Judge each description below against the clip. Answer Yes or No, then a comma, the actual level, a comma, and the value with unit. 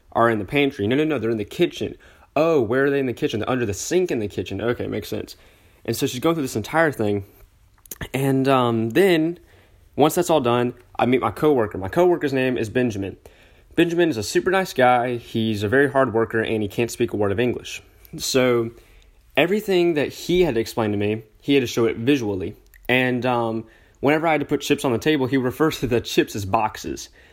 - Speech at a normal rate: No, fast, 230 wpm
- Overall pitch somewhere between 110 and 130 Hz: Yes, low, 125 Hz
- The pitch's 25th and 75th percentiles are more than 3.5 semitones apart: Yes, average, 4.6 semitones